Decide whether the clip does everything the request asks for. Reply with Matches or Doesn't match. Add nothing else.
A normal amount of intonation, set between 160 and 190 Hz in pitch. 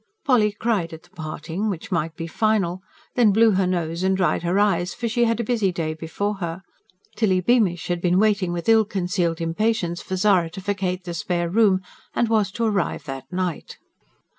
Matches